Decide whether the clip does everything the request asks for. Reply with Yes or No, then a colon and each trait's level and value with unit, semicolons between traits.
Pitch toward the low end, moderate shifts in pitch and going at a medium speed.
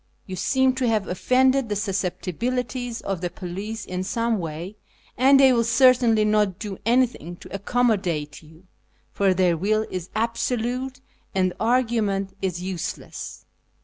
No: high, 210 Hz; average, 4.8 semitones; average, 145 wpm